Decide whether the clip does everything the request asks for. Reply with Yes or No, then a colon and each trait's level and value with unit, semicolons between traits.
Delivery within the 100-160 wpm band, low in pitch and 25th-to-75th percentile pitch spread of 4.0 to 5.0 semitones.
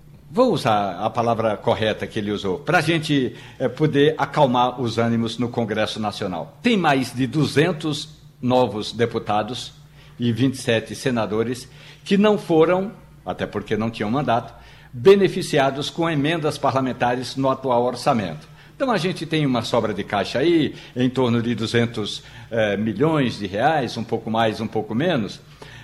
Yes: average, 150 wpm; low, 125 Hz; average, 4.6 semitones